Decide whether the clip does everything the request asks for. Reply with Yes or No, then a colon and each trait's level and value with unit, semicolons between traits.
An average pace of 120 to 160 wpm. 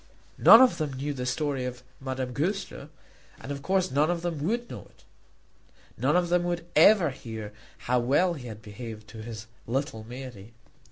No: average, 180 wpm